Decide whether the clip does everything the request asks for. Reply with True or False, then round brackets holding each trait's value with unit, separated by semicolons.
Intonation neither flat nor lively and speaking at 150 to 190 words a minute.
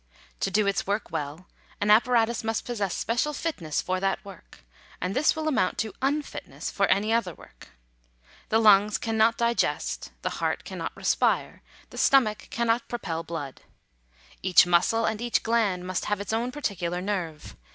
True (4.1 semitones; 170 wpm)